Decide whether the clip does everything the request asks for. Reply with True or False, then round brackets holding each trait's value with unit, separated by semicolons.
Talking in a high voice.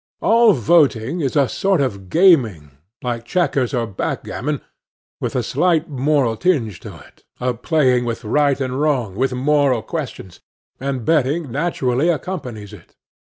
False (135 Hz)